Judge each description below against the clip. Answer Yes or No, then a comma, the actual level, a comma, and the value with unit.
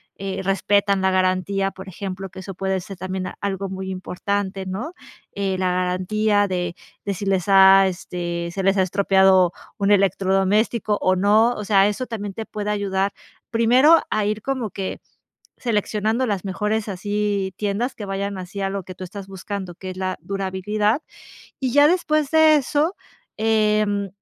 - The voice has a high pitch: Yes, high, 195 Hz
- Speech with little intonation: Yes, narrow, 1.9 semitones